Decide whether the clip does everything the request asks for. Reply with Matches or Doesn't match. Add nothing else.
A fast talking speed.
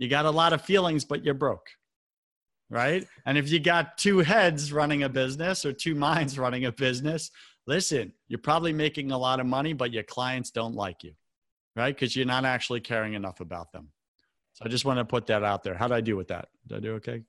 Matches